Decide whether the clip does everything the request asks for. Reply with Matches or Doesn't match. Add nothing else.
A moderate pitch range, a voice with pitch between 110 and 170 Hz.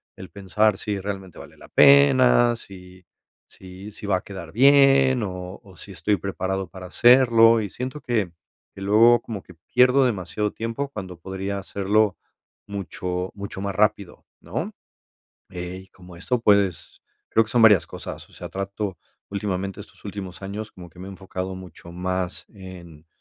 Doesn't match